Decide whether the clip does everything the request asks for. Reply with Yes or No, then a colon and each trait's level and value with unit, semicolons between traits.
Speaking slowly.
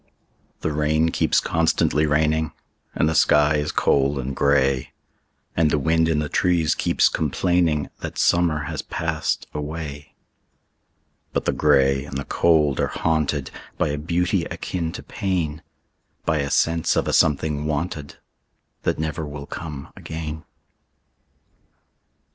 Yes: slow, 120 wpm